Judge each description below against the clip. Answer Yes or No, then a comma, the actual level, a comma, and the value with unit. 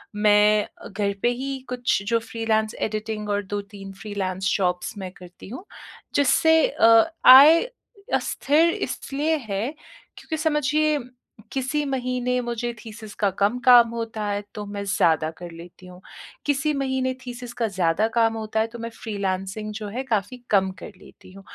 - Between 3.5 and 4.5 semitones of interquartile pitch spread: Yes, average, 4.0 semitones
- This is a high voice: Yes, high, 220 Hz